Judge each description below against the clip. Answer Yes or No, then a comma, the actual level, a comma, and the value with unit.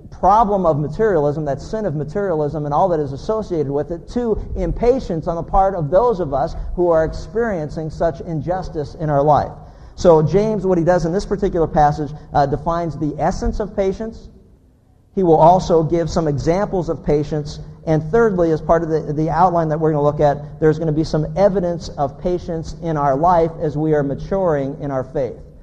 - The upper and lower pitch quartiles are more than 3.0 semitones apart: Yes, average, 3.6 semitones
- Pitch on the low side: No, medium, 160 Hz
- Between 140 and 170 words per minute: No, average, 200 wpm